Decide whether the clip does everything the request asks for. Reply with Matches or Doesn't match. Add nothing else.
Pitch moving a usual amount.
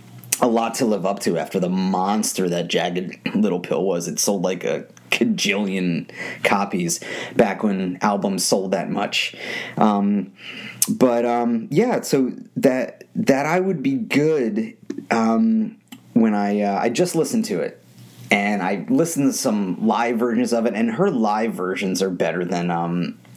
Doesn't match